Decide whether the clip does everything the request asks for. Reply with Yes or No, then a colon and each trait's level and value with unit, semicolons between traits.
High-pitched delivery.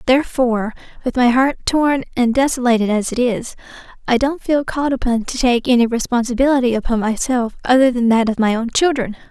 Yes: high, 245 Hz